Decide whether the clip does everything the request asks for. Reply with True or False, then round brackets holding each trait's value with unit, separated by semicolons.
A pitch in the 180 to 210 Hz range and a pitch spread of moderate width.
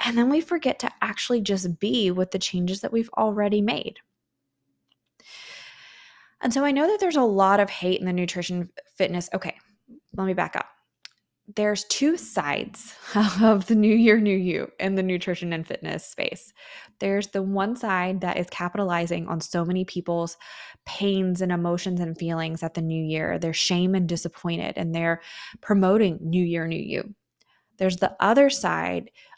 True (190 Hz; 3.1 semitones)